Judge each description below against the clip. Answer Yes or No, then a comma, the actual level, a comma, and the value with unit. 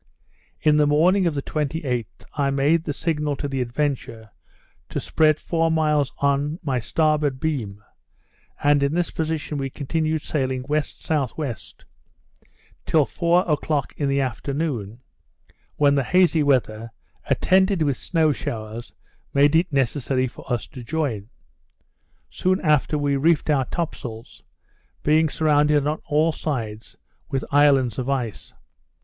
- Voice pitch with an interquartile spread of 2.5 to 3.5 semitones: Yes, average, 3.1 semitones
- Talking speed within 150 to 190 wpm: No, slow, 135 wpm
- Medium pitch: Yes, medium, 145 Hz